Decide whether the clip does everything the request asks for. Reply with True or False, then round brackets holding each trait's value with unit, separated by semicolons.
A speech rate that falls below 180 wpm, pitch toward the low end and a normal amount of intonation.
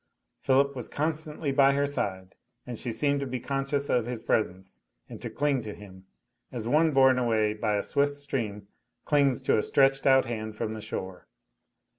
False (185 wpm; 130 Hz; 4.6 semitones)